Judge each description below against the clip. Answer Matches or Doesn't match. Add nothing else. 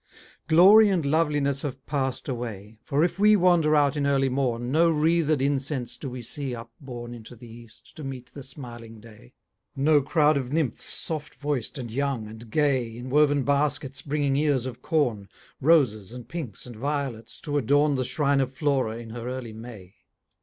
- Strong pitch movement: Doesn't match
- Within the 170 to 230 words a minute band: Matches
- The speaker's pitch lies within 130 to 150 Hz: Matches